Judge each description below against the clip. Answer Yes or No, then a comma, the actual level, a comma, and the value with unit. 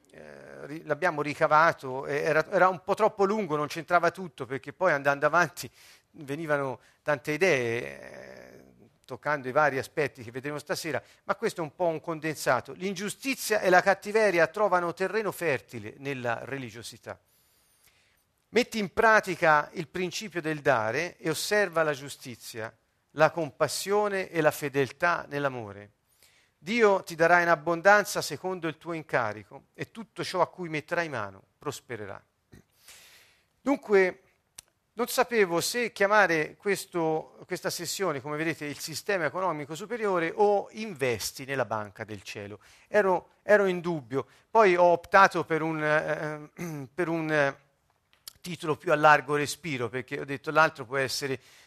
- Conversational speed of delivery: Yes, average, 135 wpm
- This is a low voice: No, medium, 155 Hz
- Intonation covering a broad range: No, average, 4.9 semitones